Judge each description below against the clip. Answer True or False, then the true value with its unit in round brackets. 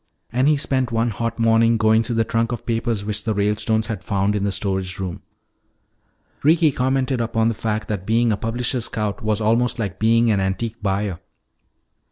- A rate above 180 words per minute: True (190 wpm)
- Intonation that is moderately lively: False (2.1 semitones)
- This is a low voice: True (115 Hz)